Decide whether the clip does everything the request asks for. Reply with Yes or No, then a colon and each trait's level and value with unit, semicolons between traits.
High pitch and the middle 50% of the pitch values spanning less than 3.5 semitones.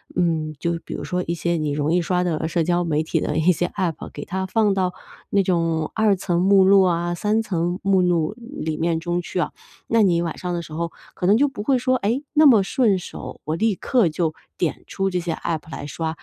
No: medium, 175 Hz; average, 3.0 semitones